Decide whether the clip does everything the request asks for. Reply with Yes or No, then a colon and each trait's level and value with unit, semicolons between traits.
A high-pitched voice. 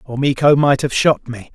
No: low, 135 Hz